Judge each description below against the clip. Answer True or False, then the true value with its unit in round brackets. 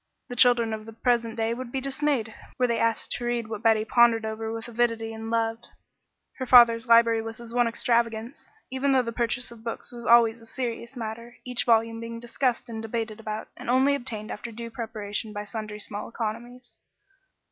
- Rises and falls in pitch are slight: True (1.3 semitones)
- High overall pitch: True (230 Hz)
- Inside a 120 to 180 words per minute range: False (195 wpm)